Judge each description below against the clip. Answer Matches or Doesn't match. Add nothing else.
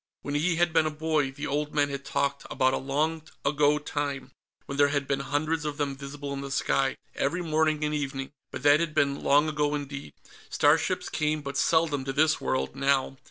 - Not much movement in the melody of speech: Matches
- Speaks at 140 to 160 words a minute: Doesn't match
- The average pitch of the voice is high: Doesn't match